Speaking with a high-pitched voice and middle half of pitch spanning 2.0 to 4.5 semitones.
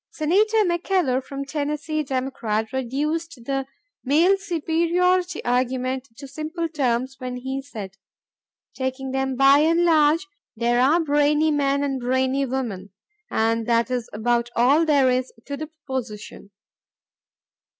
Yes: very high, 275 Hz; average, 3.6 semitones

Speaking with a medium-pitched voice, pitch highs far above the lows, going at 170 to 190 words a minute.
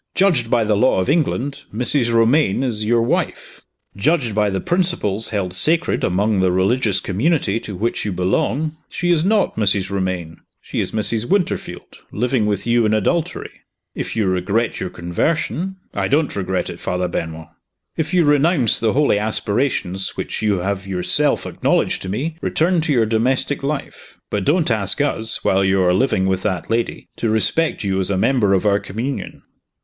No: low, 110 Hz; wide, 6.7 semitones; average, 180 wpm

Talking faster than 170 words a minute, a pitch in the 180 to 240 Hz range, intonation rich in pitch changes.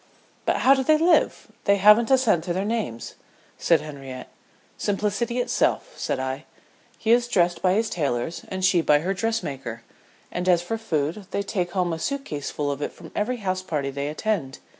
Yes: average, 195 wpm; medium, 185 Hz; wide, 6.9 semitones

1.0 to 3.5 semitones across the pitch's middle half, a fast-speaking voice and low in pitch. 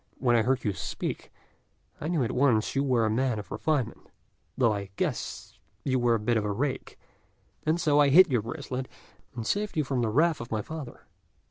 No: average, 4.4 semitones; fast, 215 wpm; low, 130 Hz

